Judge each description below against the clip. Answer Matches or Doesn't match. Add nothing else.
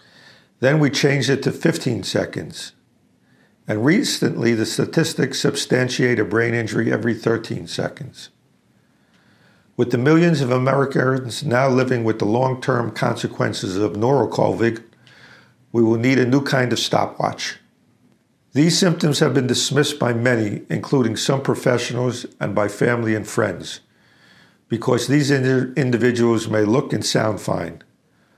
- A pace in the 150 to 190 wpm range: Doesn't match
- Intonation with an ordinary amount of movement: Matches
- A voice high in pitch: Doesn't match